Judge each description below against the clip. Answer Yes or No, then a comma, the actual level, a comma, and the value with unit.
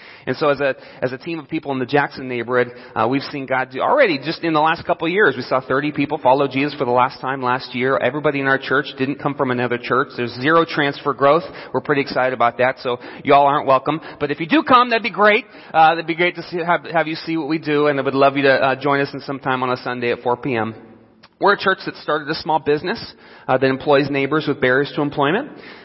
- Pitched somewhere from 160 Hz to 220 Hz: No, medium, 140 Hz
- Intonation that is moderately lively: Yes, average, 3.3 semitones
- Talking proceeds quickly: Yes, fast, 265 wpm